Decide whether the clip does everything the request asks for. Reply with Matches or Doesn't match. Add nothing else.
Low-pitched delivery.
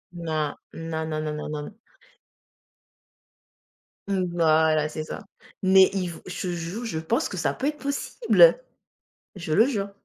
Doesn't match